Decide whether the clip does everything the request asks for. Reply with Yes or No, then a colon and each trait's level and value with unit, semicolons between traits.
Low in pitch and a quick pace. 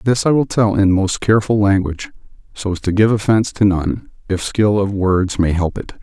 Yes: low, 100 Hz; fast, 220 wpm